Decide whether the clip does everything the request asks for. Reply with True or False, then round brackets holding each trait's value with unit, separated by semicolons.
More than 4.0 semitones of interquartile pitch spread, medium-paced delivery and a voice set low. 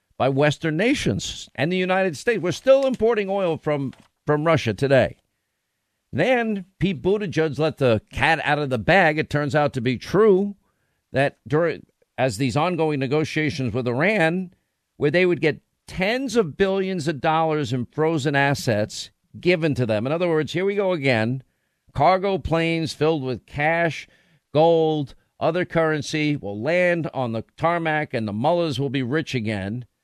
False (5.0 semitones; 160 wpm; 155 Hz)